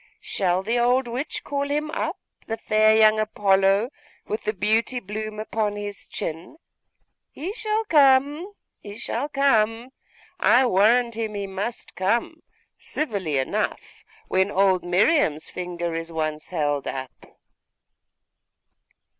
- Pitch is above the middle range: Yes, high, 215 Hz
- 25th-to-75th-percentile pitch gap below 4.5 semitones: No, average, 4.8 semitones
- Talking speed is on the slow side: Yes, slow, 125 wpm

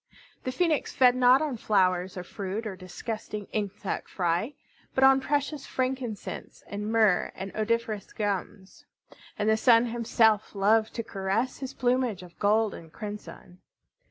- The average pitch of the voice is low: No, high, 220 Hz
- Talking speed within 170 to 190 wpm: No, average, 145 wpm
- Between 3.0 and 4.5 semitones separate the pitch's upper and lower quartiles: Yes, average, 4.1 semitones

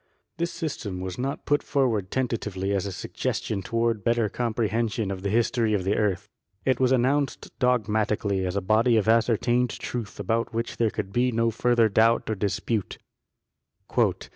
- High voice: No, low, 115 Hz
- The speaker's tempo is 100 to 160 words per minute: No, average, 170 wpm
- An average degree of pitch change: Yes, average, 3.1 semitones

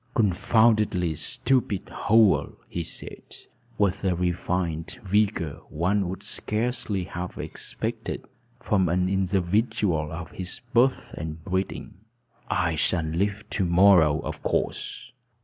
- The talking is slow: Yes, slow, 115 wpm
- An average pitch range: Yes, average, 3.2 semitones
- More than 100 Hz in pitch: No, very low, 95 Hz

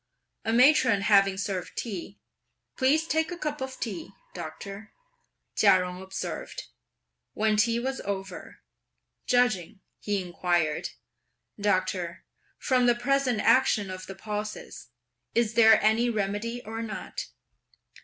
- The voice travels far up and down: No, average, 4.0 semitones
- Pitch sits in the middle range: No, high, 215 Hz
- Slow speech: Yes, slow, 120 wpm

